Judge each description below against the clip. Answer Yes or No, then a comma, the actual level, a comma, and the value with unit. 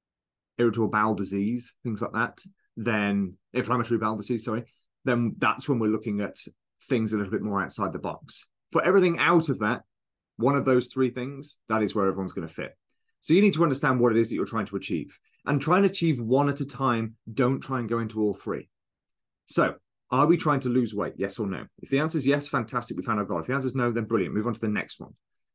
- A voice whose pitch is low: Yes, low, 120 Hz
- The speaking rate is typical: No, fast, 240 wpm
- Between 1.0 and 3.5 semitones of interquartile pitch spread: No, average, 4.2 semitones